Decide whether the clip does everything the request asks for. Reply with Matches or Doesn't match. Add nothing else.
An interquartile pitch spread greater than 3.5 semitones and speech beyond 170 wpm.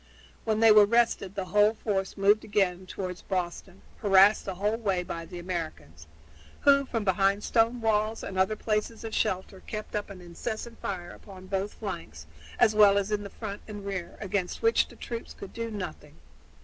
Doesn't match